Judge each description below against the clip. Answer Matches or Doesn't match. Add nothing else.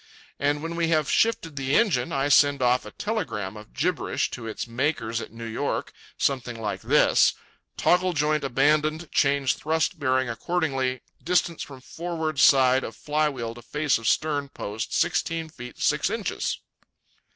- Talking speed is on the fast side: Doesn't match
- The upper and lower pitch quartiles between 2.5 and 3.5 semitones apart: Doesn't match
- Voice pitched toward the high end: Doesn't match